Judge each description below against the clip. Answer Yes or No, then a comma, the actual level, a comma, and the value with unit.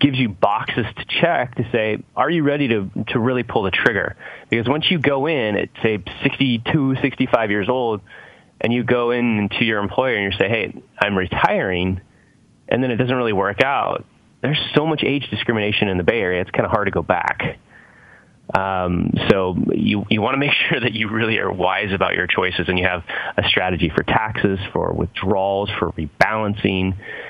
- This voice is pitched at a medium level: No, low, 110 Hz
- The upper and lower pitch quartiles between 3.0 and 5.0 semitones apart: Yes, average, 4.6 semitones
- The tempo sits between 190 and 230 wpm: Yes, average, 200 wpm